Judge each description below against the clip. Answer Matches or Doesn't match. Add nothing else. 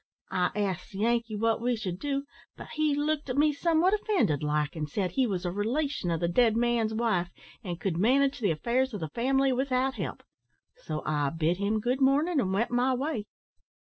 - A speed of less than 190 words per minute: Doesn't match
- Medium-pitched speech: Doesn't match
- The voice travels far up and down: Matches